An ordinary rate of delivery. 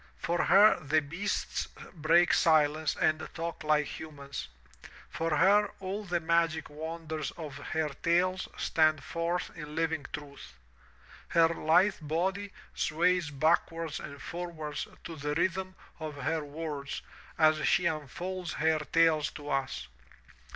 No: slow, 130 wpm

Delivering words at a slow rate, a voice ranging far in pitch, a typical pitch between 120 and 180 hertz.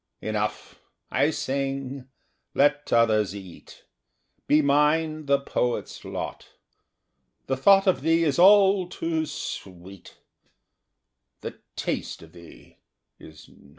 Yes: slow, 110 wpm; wide, 6.8 semitones; medium, 140 Hz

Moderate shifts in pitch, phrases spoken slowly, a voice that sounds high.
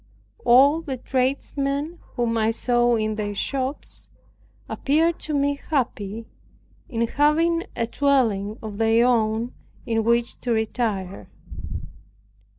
Yes: average, 4.0 semitones; slow, 115 wpm; high, 240 Hz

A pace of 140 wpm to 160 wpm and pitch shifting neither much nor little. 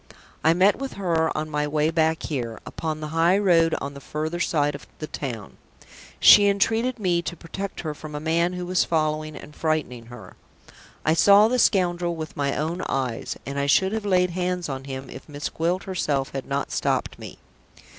No: average, 195 wpm; average, 3.6 semitones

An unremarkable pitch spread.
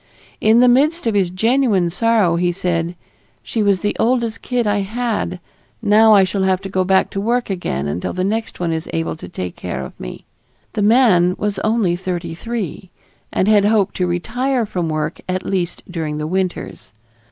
Yes: average, 4.2 semitones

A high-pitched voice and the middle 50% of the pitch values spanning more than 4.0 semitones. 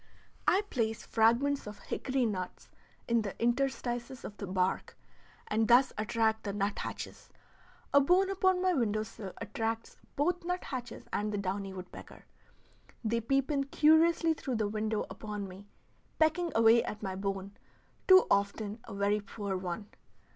Yes: high, 225 Hz; average, 5.1 semitones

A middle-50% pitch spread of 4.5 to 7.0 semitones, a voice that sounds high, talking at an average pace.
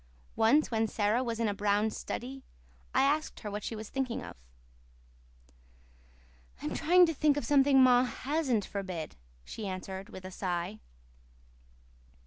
Yes: average, 5.1 semitones; high, 225 Hz; average, 145 wpm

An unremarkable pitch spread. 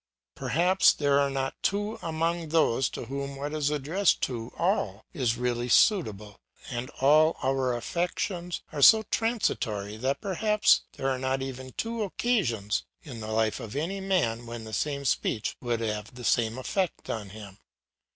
No: wide, 6.8 semitones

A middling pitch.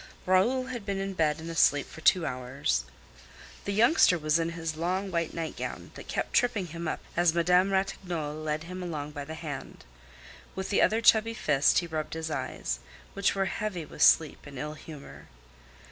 Yes: medium, 165 Hz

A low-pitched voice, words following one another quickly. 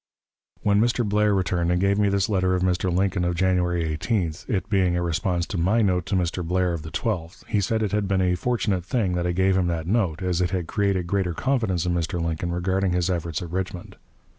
Yes: very low, 90 Hz; fast, 235 wpm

